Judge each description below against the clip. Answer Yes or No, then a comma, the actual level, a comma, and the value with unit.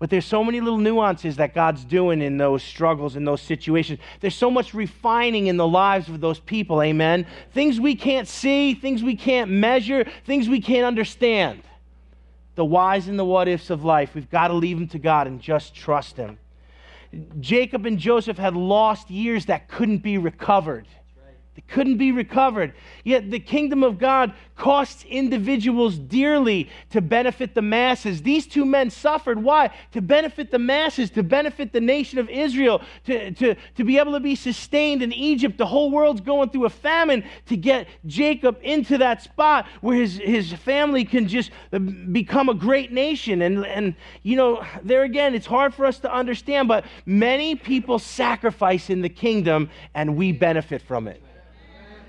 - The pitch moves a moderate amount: No, wide, 7.1 semitones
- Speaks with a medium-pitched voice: No, high, 230 Hz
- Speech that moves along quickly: No, average, 175 wpm